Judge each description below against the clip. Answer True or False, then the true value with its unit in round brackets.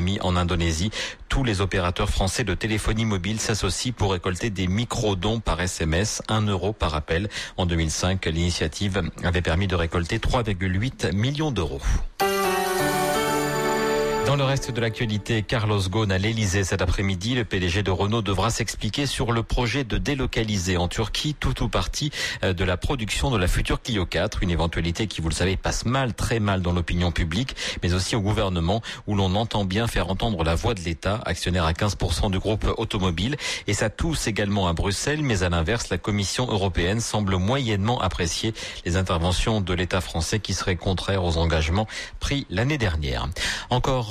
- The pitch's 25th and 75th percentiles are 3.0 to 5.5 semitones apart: True (4.1 semitones)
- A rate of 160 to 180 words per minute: True (175 wpm)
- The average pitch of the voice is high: False (100 Hz)